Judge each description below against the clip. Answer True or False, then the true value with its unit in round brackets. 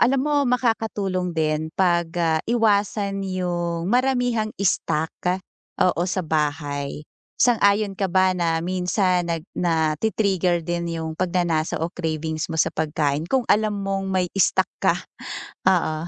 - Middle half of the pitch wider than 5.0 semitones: False (3.8 semitones)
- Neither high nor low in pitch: True (180 Hz)